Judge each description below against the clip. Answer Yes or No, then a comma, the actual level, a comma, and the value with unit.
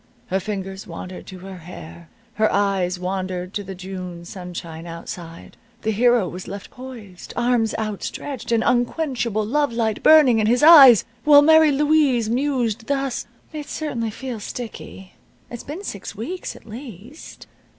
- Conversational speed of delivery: Yes, average, 150 wpm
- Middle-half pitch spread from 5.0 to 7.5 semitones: Yes, wide, 5.6 semitones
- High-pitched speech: Yes, high, 220 Hz